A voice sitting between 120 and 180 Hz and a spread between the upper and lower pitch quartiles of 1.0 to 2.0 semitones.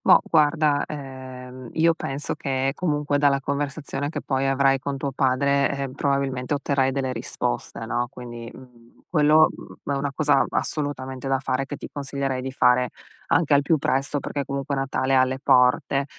Yes: low, 135 Hz; narrow, 1.6 semitones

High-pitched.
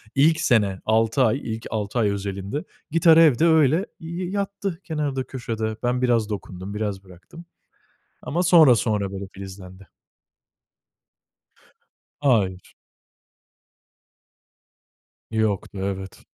No: low, 115 Hz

